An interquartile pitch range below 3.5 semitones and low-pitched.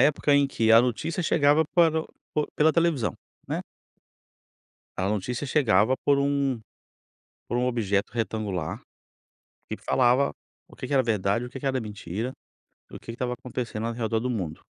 No: average, 4.1 semitones; low, 125 Hz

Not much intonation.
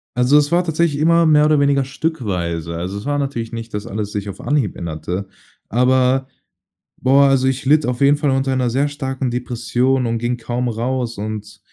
No: average, 4.0 semitones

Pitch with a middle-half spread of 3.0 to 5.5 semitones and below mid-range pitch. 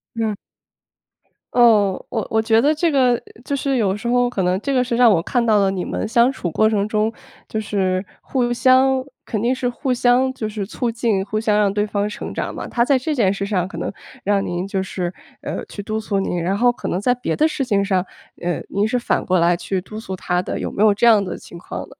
No: average, 3.9 semitones; high, 215 Hz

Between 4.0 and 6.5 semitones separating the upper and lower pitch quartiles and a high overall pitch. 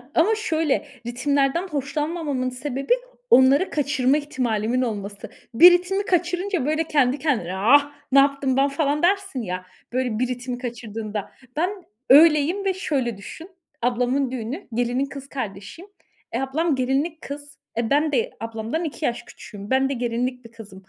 Yes: average, 4.3 semitones; very high, 270 Hz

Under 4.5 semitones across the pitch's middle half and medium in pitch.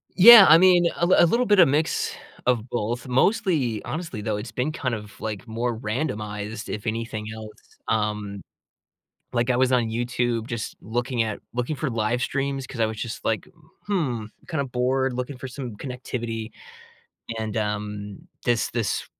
No: average, 3.6 semitones; low, 120 Hz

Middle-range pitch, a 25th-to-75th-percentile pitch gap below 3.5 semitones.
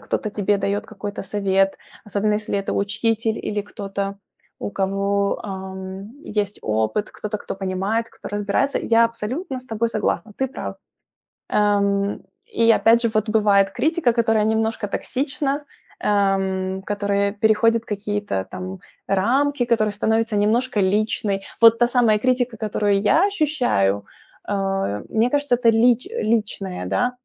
No: high, 210 Hz; narrow, 2.6 semitones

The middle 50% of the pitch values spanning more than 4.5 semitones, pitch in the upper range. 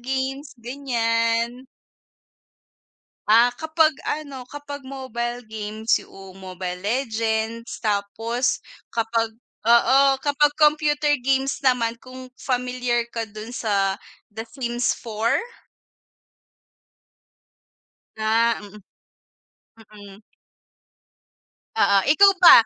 No: average, 3.3 semitones; high, 235 Hz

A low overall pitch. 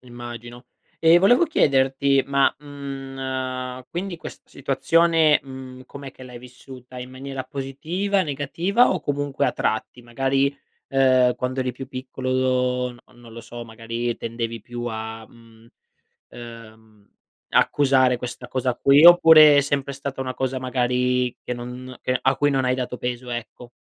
Yes: low, 130 Hz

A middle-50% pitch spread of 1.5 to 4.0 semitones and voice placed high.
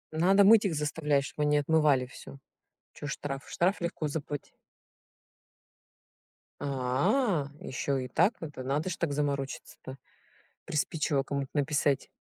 No: average, 2.8 semitones; medium, 145 Hz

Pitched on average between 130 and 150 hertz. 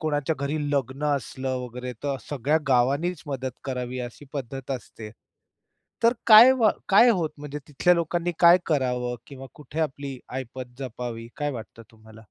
Yes: low, 135 Hz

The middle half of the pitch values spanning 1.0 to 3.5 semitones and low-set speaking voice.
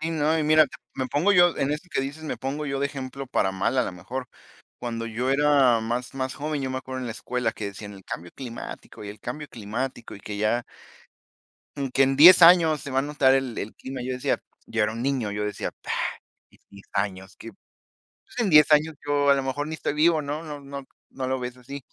No: average, 4.0 semitones; low, 130 Hz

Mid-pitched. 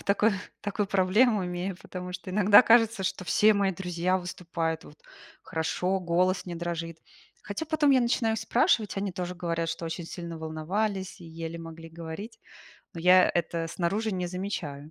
Yes: medium, 180 Hz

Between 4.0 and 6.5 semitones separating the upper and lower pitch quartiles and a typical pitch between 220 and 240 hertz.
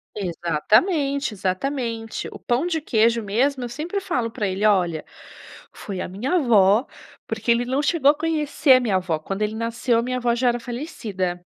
Yes: average, 5.3 semitones; high, 235 Hz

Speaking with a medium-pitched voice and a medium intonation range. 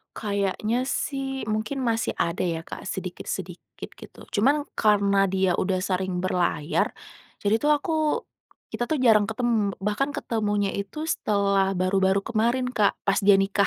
No: high, 205 Hz; average, 3.4 semitones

